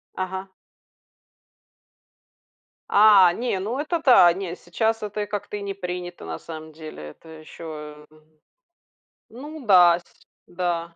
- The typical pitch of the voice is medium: Yes, medium, 180 Hz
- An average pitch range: Yes, average, 3.8 semitones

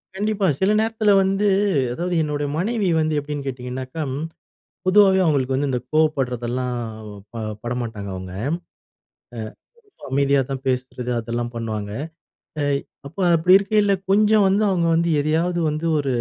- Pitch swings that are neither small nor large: No, wide, 7.1 semitones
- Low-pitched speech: No, medium, 150 Hz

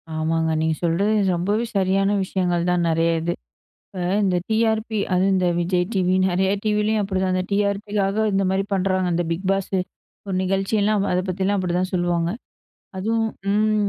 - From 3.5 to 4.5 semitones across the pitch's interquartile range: No, narrow, 2.4 semitones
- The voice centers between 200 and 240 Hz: No, high, 190 Hz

